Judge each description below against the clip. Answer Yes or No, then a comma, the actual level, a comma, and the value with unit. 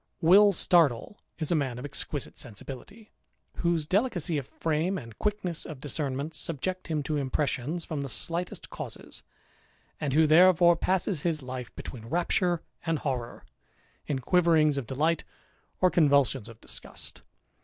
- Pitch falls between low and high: Yes, medium, 155 Hz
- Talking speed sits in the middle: Yes, average, 145 wpm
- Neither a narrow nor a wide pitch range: Yes, average, 4.2 semitones